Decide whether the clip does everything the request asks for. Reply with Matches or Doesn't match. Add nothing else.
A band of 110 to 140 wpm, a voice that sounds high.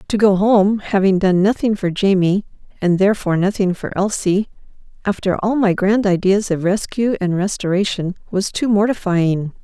Doesn't match